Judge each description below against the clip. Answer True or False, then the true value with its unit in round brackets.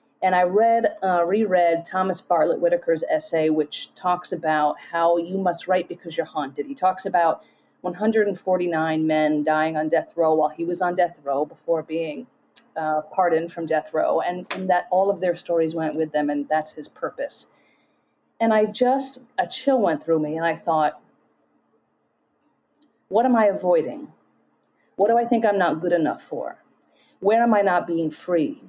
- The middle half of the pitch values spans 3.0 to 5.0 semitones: True (3.7 semitones)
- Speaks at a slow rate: False (180 wpm)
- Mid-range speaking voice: True (175 Hz)